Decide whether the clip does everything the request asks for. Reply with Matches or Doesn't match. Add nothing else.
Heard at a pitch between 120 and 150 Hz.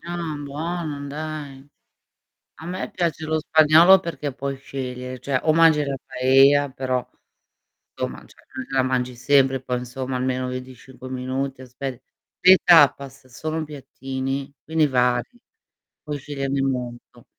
Matches